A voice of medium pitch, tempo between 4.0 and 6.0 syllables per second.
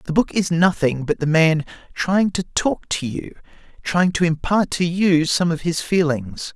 Yes: medium, 170 Hz; 4.3 syllables/s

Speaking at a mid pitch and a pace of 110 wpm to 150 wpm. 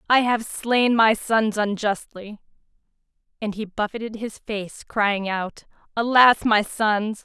No: high, 215 Hz; slow, 135 wpm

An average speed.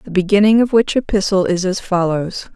Yes: average, 190 wpm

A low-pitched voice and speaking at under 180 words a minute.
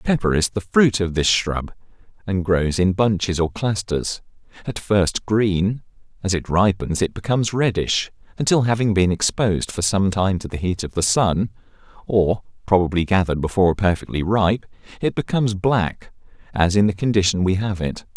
Yes: low, 100 Hz; average, 170 wpm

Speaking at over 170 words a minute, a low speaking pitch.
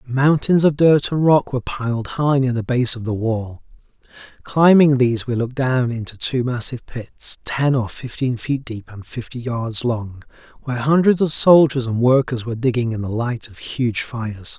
Yes: average, 190 wpm; low, 125 Hz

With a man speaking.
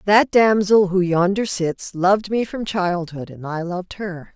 No: female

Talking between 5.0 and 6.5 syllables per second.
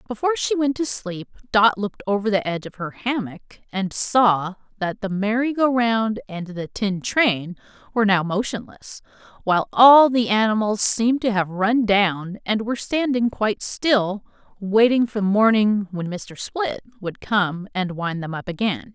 No: 4.4 syllables/s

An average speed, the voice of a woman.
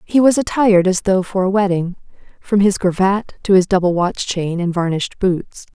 Yes: average, 195 wpm; female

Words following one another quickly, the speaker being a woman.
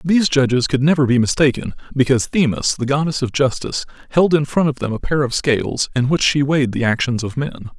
No: fast, 225 wpm; male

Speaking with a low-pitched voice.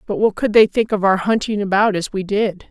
No: high, 205 Hz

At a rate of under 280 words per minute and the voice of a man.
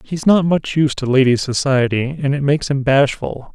Yes: fast, 205 wpm; male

